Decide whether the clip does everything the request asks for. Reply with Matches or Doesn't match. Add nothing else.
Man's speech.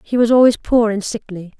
Doesn't match